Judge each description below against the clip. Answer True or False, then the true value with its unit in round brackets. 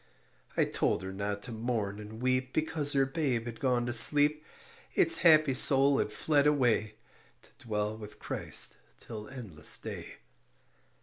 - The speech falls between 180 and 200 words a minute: False (150 wpm)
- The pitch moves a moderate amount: True (4.8 semitones)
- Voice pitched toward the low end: True (125 Hz)